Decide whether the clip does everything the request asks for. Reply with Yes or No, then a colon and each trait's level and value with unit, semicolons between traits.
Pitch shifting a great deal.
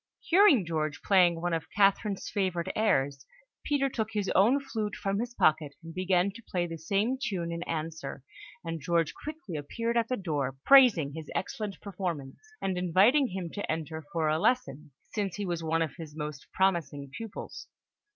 No: average, 4.7 semitones